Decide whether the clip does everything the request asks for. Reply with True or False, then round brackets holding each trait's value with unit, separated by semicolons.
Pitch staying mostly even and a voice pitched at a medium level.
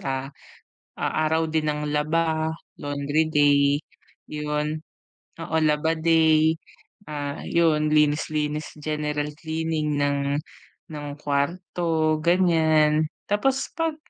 True (1.3 semitones; 155 Hz)